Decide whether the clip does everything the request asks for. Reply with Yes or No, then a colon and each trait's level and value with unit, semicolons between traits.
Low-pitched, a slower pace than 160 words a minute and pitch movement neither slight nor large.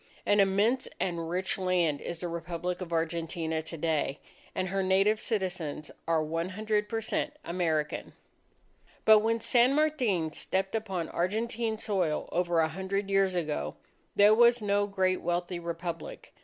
No: medium, 185 Hz; average, 150 wpm; average, 3.8 semitones